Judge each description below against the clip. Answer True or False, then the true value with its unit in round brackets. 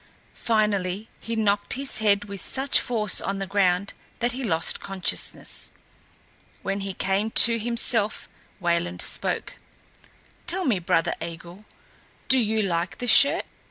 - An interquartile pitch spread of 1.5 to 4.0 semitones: True (3.4 semitones)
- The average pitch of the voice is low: False (205 Hz)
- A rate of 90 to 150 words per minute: True (135 wpm)